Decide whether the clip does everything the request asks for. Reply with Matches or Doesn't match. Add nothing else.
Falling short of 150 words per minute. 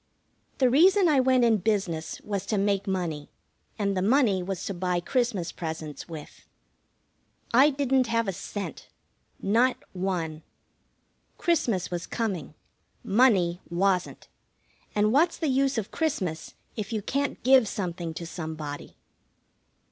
Matches